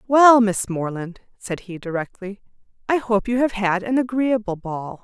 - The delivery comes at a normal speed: Yes, average, 165 wpm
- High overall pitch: Yes, high, 210 Hz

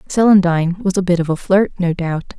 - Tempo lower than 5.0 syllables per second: No, 5.9 syllables/s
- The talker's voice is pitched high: No, medium, 180 Hz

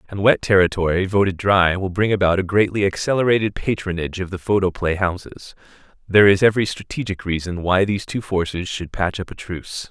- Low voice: Yes, very low, 95 Hz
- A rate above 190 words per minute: No, average, 180 wpm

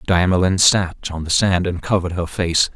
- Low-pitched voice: Yes, very low, 90 Hz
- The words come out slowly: No, average, 195 wpm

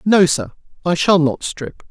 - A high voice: No, medium, 160 Hz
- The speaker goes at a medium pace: Yes, average, 190 wpm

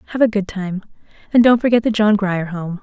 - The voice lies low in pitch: No, high, 205 Hz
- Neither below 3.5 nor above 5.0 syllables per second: No, 5.9 syllables/s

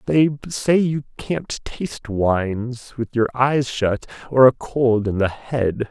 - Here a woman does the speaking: No, male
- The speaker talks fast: No, average, 160 wpm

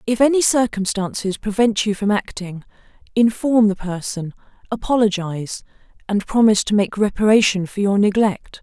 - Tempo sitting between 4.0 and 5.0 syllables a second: No, 5.2 syllables/s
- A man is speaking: No, female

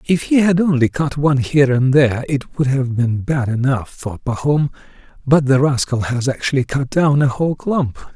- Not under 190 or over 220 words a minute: Yes, average, 200 wpm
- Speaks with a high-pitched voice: No, low, 135 Hz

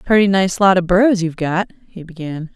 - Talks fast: Yes, fast, 210 wpm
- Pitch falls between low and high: Yes, medium, 180 Hz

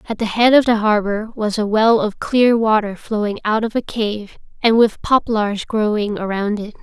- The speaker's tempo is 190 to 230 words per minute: Yes, average, 200 wpm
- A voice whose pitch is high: Yes, high, 215 Hz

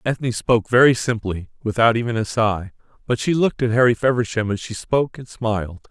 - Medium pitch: No, low, 115 Hz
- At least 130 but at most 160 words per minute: No, average, 195 wpm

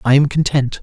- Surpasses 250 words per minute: No, fast, 220 wpm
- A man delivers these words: Yes, male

